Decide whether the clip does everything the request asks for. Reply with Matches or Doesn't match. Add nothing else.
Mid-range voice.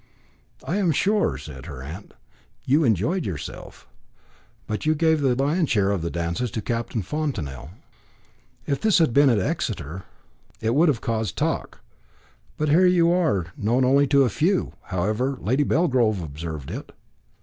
Doesn't match